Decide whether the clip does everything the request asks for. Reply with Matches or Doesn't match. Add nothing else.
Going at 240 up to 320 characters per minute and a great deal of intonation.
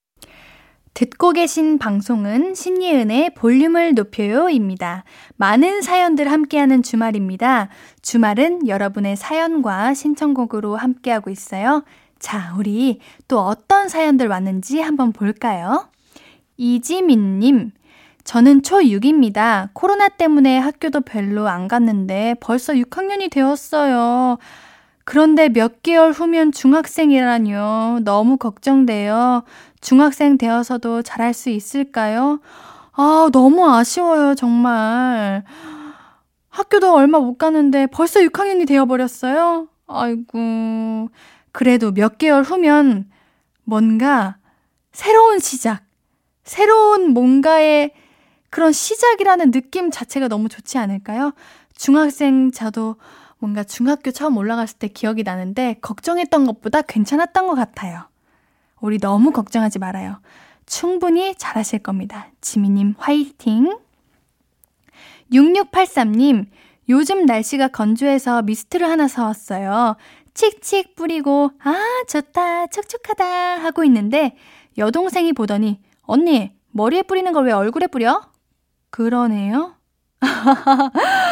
Matches